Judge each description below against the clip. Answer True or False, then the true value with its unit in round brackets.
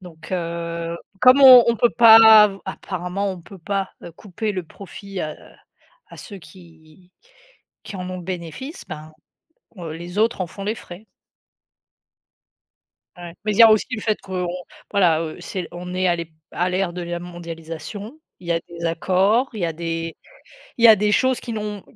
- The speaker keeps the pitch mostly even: False (3.7 semitones)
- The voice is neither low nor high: True (180 Hz)